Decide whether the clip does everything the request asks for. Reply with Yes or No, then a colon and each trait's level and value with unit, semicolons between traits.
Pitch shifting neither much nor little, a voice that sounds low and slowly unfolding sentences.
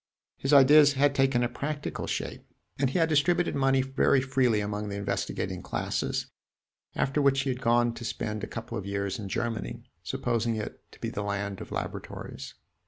No: average, 4.5 semitones; low, 120 Hz; average, 180 wpm